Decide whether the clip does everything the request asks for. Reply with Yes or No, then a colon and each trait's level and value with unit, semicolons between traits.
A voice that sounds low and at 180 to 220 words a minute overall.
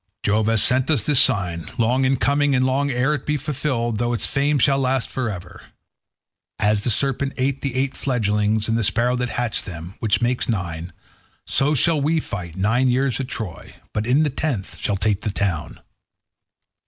Yes: low, 120 Hz; average, 190 wpm